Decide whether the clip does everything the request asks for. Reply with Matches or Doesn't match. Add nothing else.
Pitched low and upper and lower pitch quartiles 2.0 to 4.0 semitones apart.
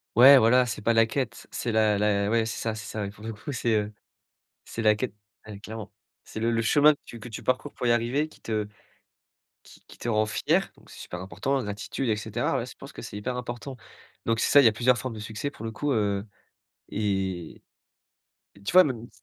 Matches